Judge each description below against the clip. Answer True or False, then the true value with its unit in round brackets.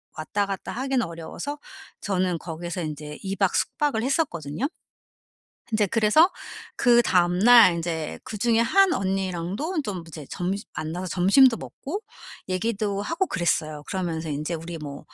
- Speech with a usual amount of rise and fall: False (5.7 semitones)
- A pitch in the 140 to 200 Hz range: True (190 Hz)